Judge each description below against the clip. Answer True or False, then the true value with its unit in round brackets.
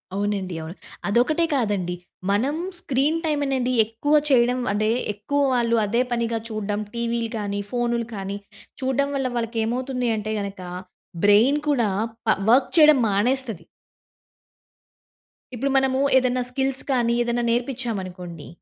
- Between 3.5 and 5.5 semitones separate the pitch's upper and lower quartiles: True (4.2 semitones)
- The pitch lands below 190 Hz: False (235 Hz)